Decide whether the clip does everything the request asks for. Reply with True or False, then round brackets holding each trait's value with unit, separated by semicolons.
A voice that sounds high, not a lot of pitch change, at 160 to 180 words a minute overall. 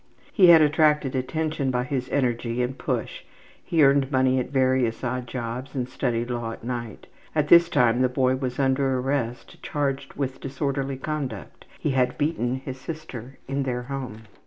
False (130 Hz; 2.1 semitones; 170 wpm)